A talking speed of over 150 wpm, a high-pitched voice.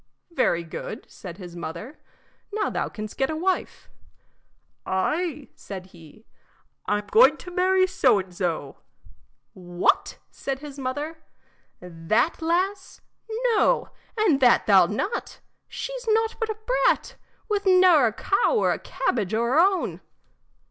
No: average, 140 wpm; very high, 275 Hz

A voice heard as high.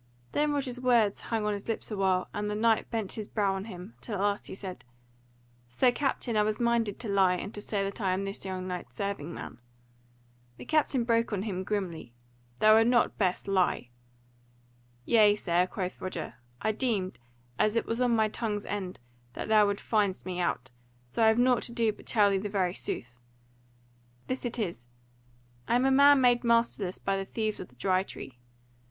Yes: high, 205 Hz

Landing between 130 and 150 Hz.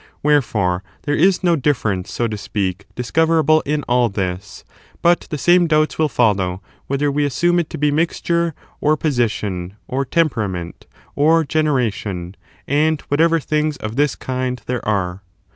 Yes: medium, 140 Hz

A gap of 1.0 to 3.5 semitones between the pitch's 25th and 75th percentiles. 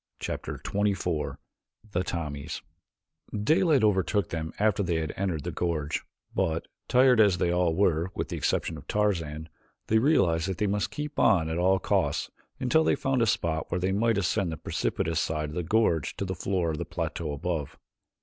No: average, 4.4 semitones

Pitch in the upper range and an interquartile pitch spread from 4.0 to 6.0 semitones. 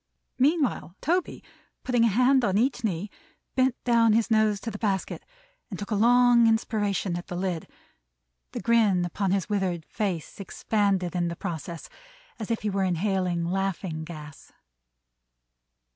Yes: high, 200 Hz; average, 4.3 semitones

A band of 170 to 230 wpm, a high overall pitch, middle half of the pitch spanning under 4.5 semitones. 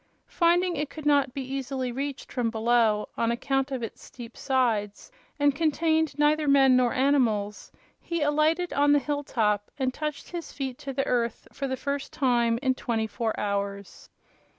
Yes: average, 175 wpm; very high, 265 Hz; average, 3.7 semitones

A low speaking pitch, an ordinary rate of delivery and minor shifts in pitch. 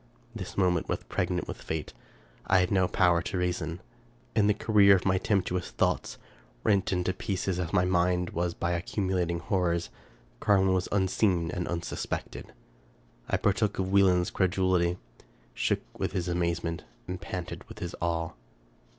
Yes: very low, 90 Hz; average, 155 wpm; narrow, 1.8 semitones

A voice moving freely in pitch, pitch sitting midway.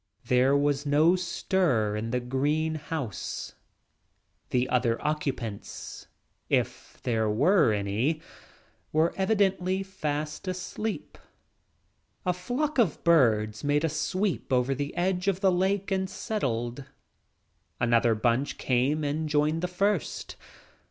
Yes: wide, 6.6 semitones; medium, 150 Hz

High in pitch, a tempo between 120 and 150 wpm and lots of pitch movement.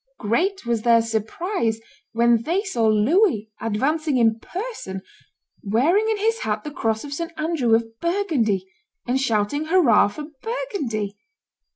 Yes: high, 245 Hz; average, 140 wpm; wide, 7.8 semitones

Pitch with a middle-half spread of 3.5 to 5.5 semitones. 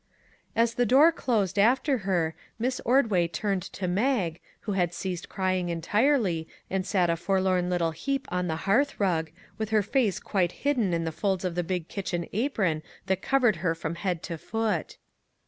Yes: average, 4.4 semitones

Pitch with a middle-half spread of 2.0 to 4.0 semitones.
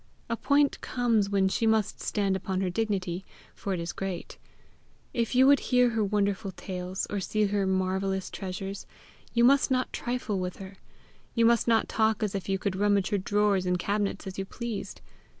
Yes: average, 2.9 semitones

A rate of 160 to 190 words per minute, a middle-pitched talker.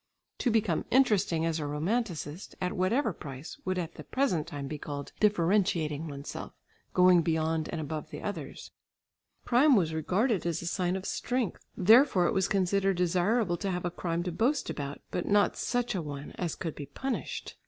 Yes: average, 180 wpm; medium, 180 Hz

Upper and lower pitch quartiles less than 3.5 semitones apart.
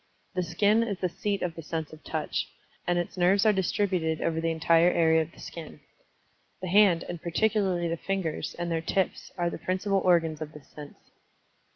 Yes: average, 2.8 semitones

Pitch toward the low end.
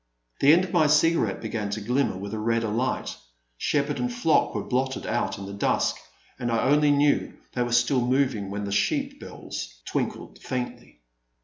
Yes: low, 125 Hz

